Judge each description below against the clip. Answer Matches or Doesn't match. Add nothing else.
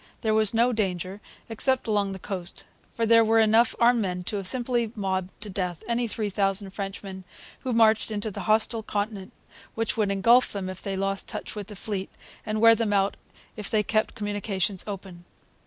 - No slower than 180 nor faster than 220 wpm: Matches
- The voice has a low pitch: Doesn't match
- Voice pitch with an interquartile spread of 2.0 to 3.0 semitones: Matches